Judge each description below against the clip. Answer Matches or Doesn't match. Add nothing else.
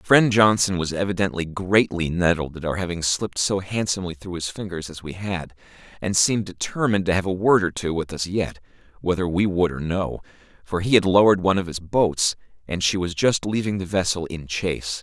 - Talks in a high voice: Doesn't match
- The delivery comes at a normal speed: Doesn't match